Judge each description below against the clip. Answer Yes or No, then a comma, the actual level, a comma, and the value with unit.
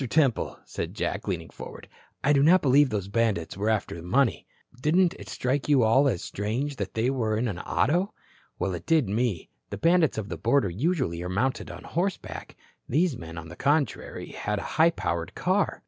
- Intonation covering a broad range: Yes, wide, 6.7 semitones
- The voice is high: No, low, 125 Hz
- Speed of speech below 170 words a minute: No, average, 195 wpm